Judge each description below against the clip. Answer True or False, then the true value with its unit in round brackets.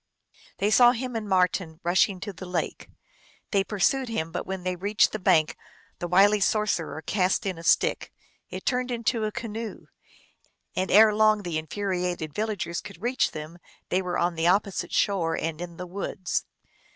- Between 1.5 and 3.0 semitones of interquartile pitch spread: False (3.4 semitones)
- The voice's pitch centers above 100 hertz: True (190 Hz)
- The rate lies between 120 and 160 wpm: False (175 wpm)